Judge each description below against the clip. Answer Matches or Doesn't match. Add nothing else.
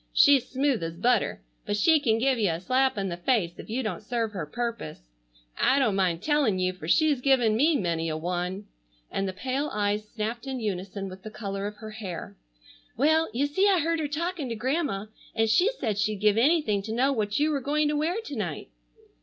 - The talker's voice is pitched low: Doesn't match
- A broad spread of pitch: Matches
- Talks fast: Matches